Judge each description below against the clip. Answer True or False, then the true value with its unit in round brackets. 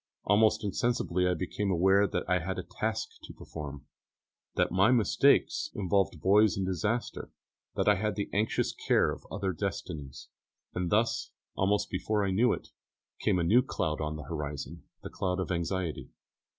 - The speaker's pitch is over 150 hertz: False (95 Hz)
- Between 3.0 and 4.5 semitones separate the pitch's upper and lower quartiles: True (3.3 semitones)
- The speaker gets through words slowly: False (165 wpm)